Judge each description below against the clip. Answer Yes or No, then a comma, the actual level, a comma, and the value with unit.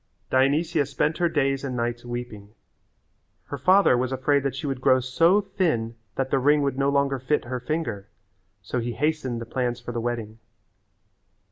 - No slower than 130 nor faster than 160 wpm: No, average, 175 wpm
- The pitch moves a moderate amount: Yes, average, 3.4 semitones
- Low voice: Yes, low, 130 Hz